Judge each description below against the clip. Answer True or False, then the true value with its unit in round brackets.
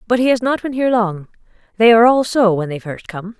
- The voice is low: False (220 Hz)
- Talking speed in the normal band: False (265 wpm)